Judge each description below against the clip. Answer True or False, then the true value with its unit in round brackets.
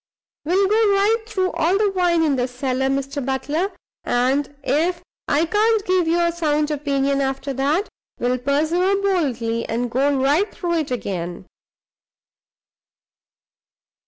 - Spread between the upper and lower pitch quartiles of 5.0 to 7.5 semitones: True (5.4 semitones)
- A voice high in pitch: True (295 Hz)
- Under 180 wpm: True (135 wpm)